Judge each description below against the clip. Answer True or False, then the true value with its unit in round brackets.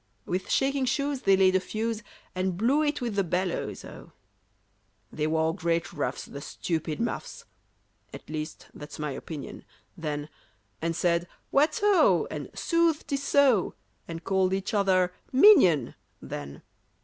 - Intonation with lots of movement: True (7.8 semitones)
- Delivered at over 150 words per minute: False (145 wpm)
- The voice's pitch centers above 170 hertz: True (190 Hz)